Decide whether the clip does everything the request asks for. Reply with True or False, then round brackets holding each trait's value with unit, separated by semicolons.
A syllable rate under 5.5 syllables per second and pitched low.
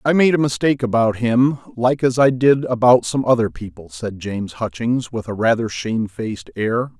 True (5.1 syllables/s; 120 Hz)